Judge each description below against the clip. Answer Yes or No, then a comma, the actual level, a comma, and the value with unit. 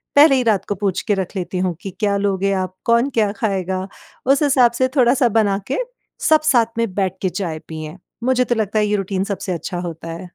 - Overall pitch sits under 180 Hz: No, high, 200 Hz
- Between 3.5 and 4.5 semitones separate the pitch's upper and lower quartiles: Yes, average, 4.2 semitones